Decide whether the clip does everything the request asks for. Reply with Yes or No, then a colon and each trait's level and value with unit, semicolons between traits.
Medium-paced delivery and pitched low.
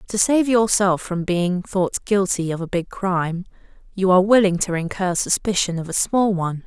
No: average, 190 wpm; high, 190 Hz